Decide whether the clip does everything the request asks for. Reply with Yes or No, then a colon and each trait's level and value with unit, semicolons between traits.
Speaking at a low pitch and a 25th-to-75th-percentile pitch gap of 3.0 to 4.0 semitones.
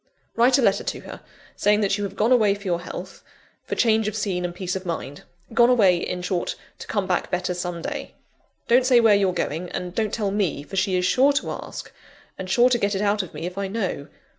No: high, 195 Hz; average, 3.4 semitones